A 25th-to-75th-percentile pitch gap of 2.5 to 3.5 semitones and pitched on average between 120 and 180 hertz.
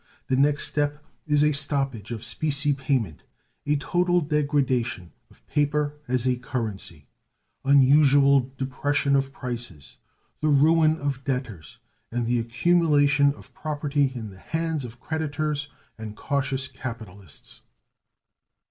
Yes: average, 3.2 semitones; medium, 140 Hz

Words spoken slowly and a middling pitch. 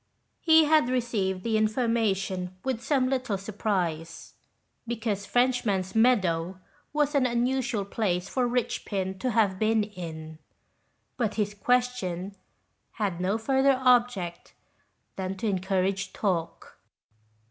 No: slow, 115 wpm; high, 215 Hz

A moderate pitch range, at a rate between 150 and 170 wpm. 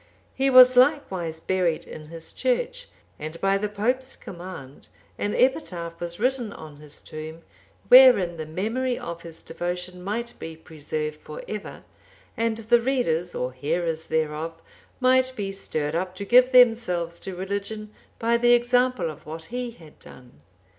No: wide, 6.9 semitones; average, 155 wpm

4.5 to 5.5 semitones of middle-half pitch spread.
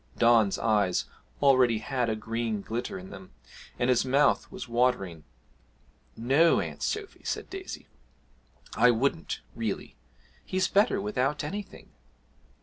Yes: average, 4.9 semitones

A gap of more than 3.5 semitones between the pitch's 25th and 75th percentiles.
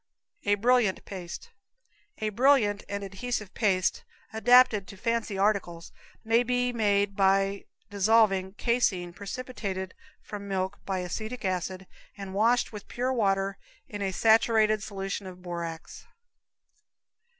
No: average, 2.9 semitones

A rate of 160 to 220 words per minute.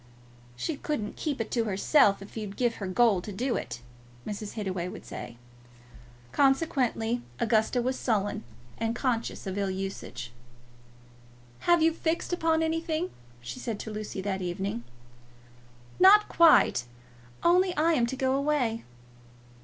No: average, 140 wpm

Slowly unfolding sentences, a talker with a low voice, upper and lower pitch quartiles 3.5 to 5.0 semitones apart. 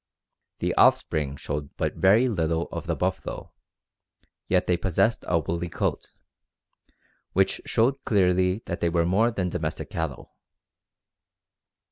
No: slow, 125 wpm; very low, 90 Hz; average, 2.9 semitones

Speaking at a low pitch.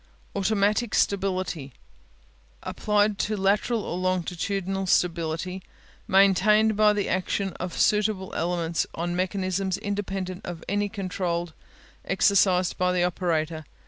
No: high, 190 Hz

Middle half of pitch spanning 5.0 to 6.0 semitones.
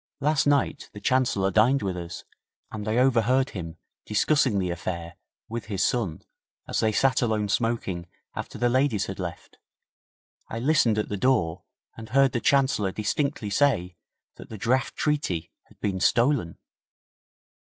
Yes: wide, 5.5 semitones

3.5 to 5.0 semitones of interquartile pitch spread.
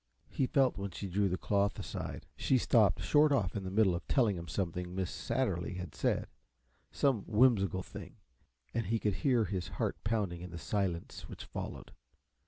Yes: average, 4.1 semitones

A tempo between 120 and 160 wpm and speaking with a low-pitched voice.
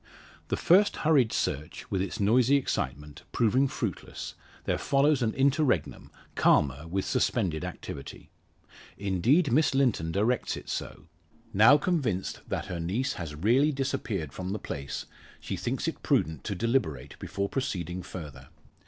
Yes: average, 140 wpm; low, 100 Hz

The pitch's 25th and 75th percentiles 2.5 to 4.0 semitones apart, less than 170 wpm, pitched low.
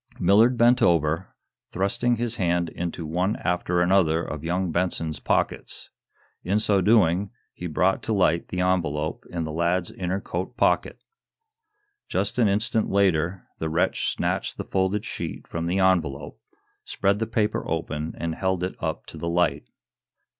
Yes: average, 2.9 semitones; average, 155 wpm; very low, 90 Hz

